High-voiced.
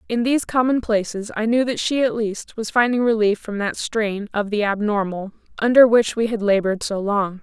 Yes: high, 220 Hz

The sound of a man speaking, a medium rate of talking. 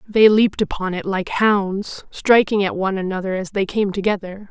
No: female; average, 185 wpm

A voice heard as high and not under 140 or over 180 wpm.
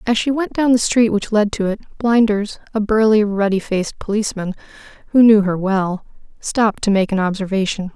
No: high, 210 Hz; average, 190 wpm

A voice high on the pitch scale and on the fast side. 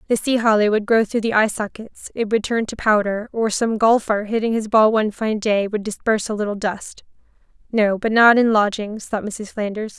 Yes: high, 215 Hz; fast, 210 wpm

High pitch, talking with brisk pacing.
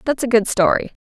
Yes: high, 230 Hz; fast, 235 wpm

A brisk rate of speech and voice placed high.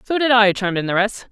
Yes: fast, 320 wpm; high, 215 Hz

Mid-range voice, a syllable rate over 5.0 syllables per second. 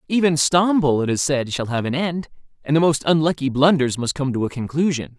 Yes: medium, 145 Hz; 5.5 syllables/s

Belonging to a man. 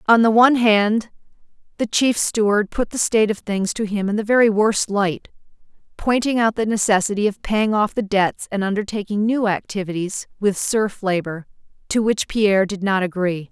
No: female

